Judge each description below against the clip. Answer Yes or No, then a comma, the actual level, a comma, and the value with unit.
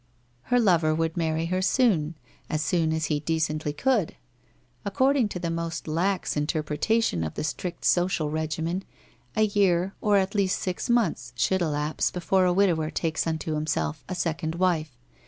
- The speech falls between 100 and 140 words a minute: No, average, 160 wpm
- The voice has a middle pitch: Yes, medium, 165 Hz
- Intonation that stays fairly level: No, average, 3.4 semitones